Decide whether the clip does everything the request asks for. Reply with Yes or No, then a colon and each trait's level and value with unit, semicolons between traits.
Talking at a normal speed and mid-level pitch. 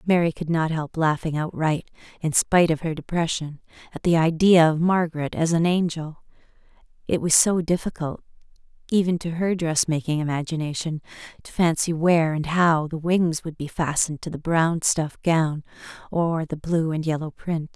Yes: average, 170 wpm; medium, 160 Hz